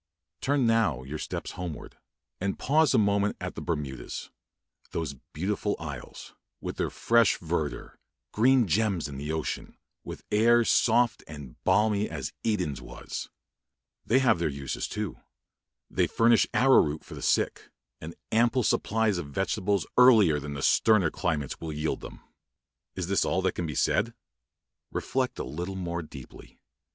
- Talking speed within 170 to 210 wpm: No, average, 155 wpm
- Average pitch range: No, wide, 6.6 semitones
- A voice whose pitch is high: No, very low, 95 Hz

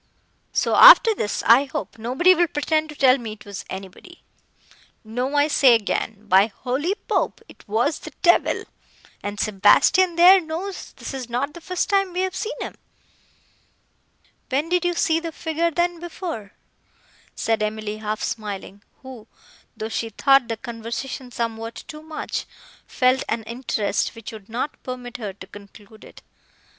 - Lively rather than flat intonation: Yes, wide, 7.0 semitones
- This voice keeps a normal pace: Yes, average, 160 wpm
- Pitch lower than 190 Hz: No, very high, 255 Hz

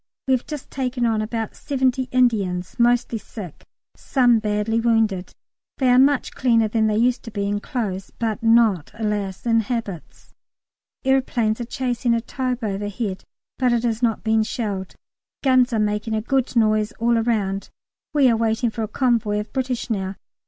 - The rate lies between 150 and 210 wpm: Yes, average, 170 wpm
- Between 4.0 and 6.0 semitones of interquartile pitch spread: No, average, 2.8 semitones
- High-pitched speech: Yes, high, 225 Hz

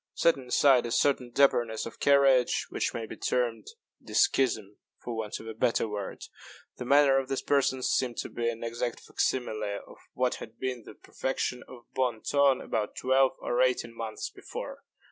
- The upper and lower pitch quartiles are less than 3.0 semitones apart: Yes, narrow, 2.6 semitones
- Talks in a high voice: No, low, 125 Hz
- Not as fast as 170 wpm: No, average, 180 wpm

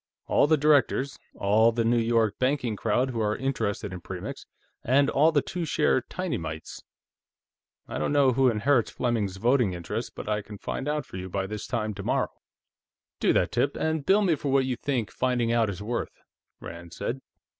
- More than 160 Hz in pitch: No, low, 120 Hz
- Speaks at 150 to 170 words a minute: No, average, 190 wpm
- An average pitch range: Yes, average, 4.7 semitones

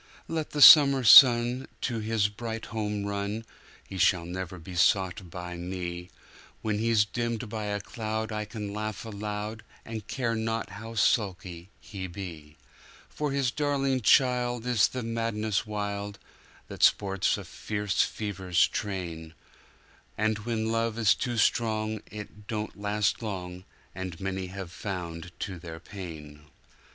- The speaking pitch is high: No, low, 105 Hz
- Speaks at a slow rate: Yes, slow, 125 wpm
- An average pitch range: Yes, average, 3.3 semitones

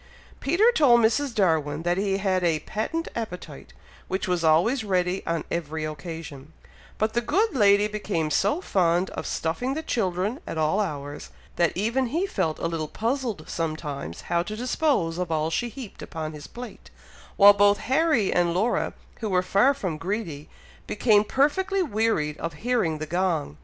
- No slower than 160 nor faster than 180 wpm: Yes, average, 170 wpm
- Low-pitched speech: No, high, 190 Hz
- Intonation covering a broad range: Yes, wide, 6.2 semitones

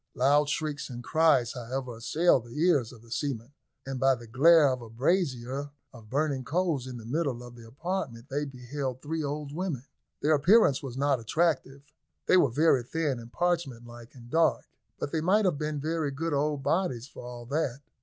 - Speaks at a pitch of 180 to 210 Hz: No, medium, 140 Hz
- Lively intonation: No, average, 4.3 semitones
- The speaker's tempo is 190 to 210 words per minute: Yes, average, 195 wpm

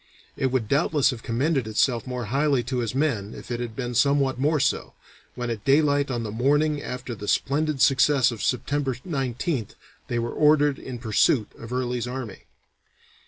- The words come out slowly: No, average, 175 wpm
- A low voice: Yes, low, 130 Hz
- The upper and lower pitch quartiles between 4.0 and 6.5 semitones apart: No, average, 3.1 semitones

